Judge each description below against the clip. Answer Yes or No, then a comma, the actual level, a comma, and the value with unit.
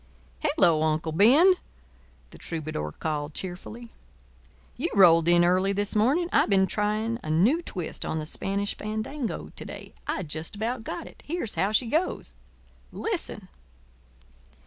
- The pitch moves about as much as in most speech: No, wide, 5.8 semitones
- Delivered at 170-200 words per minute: No, average, 140 wpm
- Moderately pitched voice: No, high, 200 Hz